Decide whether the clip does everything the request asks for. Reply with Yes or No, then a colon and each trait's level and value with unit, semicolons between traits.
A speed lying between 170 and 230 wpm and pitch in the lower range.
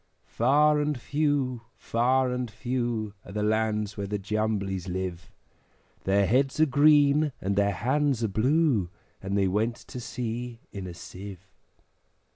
No: average, 145 wpm; low, 115 Hz